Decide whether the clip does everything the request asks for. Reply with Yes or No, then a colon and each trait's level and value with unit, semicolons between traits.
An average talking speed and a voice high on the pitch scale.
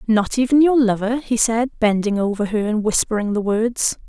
Yes: average, 190 wpm; high, 225 Hz